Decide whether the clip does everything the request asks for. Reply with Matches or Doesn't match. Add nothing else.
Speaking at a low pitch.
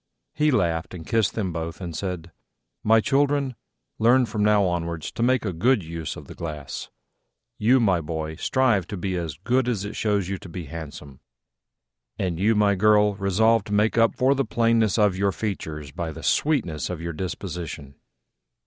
Matches